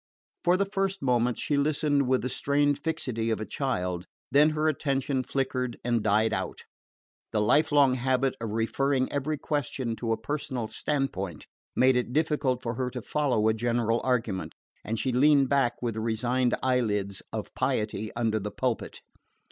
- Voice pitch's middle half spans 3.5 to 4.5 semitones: Yes, average, 3.8 semitones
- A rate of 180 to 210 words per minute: No, average, 170 wpm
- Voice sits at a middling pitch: No, low, 125 Hz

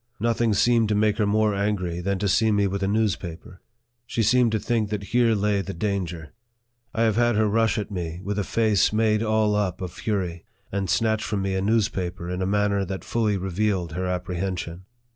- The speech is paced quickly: Yes, fast, 210 wpm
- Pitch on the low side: Yes, low, 100 Hz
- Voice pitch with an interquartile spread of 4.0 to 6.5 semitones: No, average, 2.7 semitones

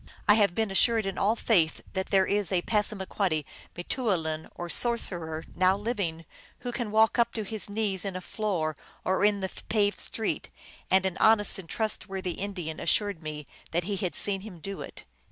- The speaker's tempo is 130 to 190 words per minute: No, average, 200 wpm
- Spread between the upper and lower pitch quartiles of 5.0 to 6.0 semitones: No, average, 3.5 semitones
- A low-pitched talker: No, high, 195 Hz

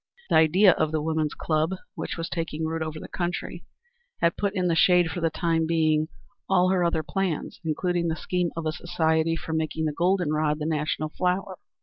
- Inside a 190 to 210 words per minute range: Yes, fast, 205 wpm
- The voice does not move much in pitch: Yes, narrow, 2.1 semitones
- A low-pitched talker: No, medium, 165 Hz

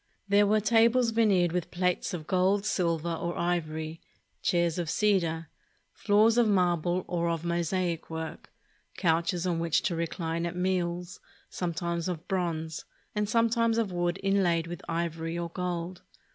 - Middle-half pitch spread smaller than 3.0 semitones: Yes, narrow, 2.4 semitones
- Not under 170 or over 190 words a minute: No, average, 145 wpm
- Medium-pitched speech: Yes, medium, 175 Hz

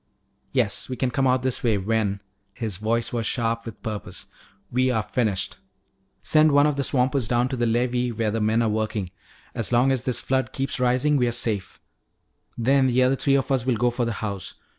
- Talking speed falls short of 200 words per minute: No, fast, 205 wpm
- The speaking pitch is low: Yes, low, 120 Hz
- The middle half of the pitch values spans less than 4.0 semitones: Yes, average, 2.8 semitones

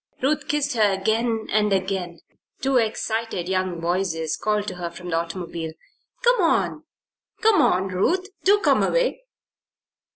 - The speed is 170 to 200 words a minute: No, average, 140 wpm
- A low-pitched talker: No, high, 195 Hz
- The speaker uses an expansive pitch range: Yes, wide, 6.5 semitones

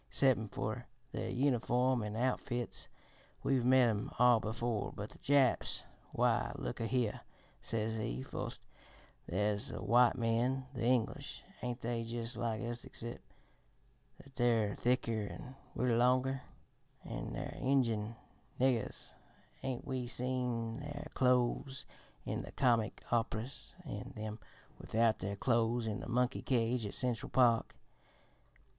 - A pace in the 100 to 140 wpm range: Yes, slow, 135 wpm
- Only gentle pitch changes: Yes, narrow, 2.1 semitones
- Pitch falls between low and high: No, low, 120 Hz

